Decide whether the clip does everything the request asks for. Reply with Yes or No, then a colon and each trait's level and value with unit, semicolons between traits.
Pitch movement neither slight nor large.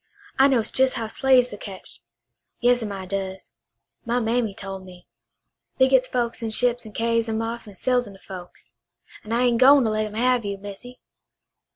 Yes: average, 3.5 semitones